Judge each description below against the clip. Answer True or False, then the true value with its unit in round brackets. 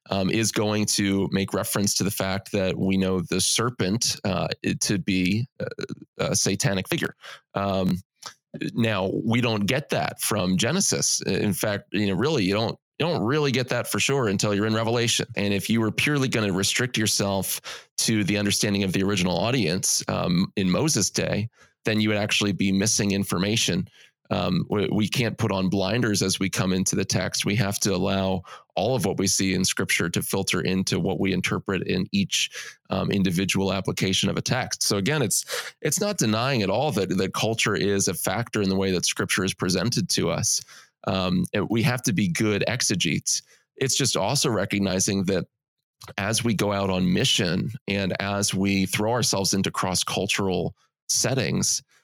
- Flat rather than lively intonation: False (3.2 semitones)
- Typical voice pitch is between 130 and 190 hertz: False (100 Hz)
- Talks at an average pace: True (185 wpm)